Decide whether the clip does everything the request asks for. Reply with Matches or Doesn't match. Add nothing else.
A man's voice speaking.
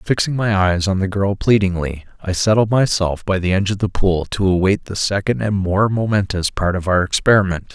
Matches